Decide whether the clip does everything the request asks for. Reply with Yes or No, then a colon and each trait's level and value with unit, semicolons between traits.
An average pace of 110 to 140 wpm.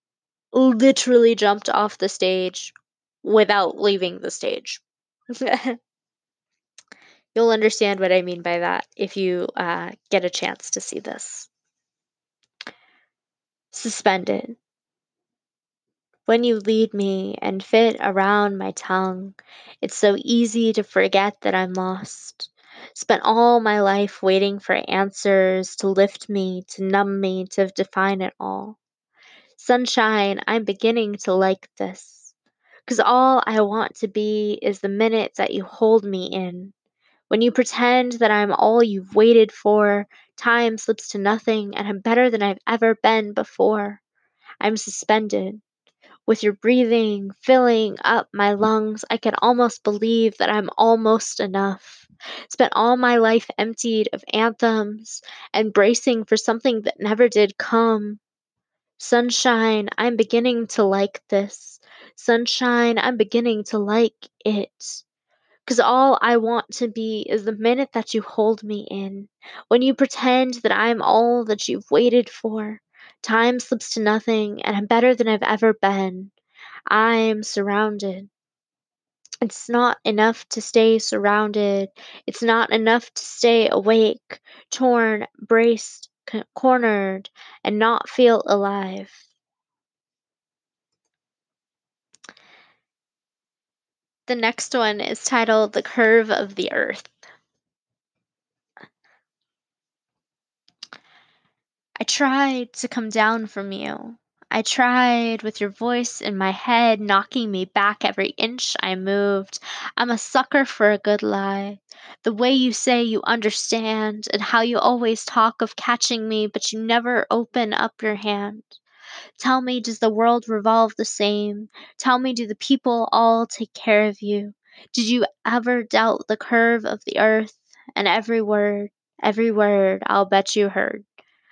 Yes: slow, 135 wpm